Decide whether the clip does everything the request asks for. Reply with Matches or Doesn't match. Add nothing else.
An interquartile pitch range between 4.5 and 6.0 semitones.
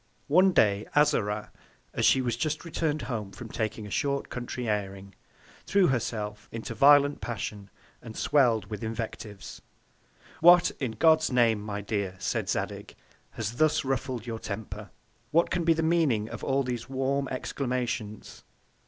Matches